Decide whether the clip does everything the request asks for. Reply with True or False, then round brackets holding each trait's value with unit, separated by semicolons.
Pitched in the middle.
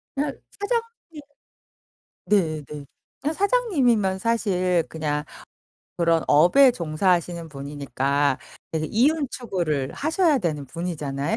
True (180 Hz)